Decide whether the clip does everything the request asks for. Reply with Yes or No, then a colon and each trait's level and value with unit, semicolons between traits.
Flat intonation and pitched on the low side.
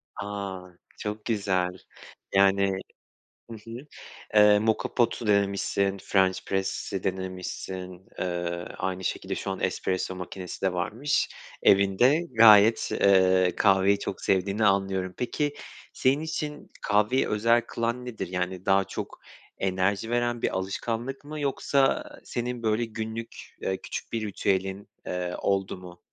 No: average, 3.4 semitones; low, 100 Hz